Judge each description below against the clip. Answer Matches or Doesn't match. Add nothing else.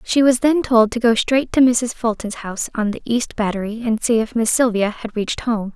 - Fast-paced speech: Matches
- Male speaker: Doesn't match